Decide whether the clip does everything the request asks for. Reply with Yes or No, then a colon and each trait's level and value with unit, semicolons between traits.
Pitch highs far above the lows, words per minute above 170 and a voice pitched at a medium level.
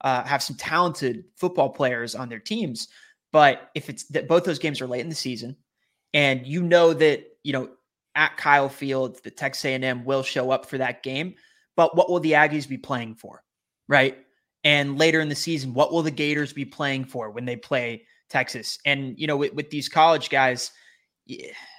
No: average, 3.8 semitones; average, 200 wpm; medium, 145 Hz